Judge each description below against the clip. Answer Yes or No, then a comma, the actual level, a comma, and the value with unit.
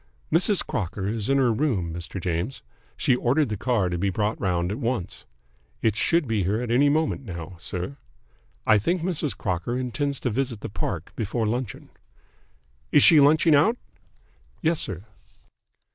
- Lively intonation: Yes, wide, 6.7 semitones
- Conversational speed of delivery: Yes, average, 165 wpm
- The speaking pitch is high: No, low, 115 Hz